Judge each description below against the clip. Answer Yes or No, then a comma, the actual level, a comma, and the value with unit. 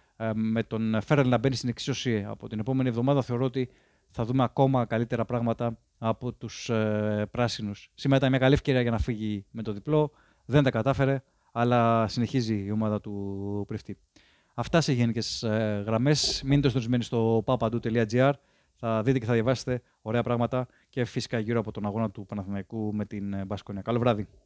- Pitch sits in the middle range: No, low, 115 Hz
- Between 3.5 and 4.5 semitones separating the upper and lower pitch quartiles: No, average, 3.0 semitones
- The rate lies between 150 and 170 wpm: Yes, average, 165 wpm